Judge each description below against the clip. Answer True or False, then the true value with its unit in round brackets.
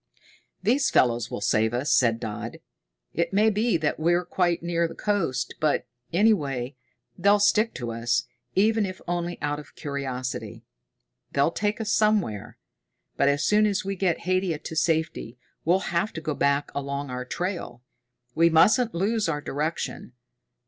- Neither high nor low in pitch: True (165 Hz)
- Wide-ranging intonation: True (6.1 semitones)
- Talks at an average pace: True (160 wpm)